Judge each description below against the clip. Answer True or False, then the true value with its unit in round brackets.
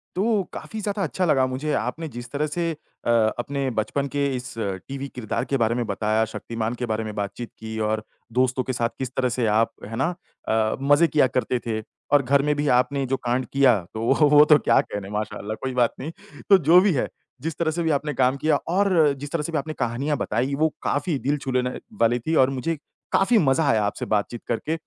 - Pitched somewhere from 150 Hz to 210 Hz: False (130 Hz)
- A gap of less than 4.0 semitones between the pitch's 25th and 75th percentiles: False (4.5 semitones)